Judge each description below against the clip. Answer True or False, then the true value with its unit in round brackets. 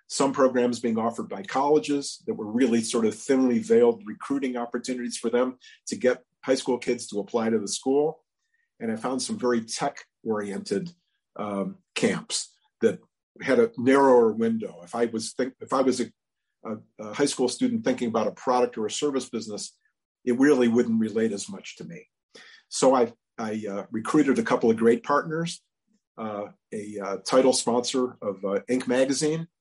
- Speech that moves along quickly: False (180 wpm)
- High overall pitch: False (125 Hz)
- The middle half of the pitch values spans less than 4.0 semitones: False (4.7 semitones)